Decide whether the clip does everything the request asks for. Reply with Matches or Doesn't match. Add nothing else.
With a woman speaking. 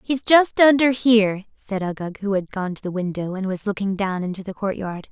Matches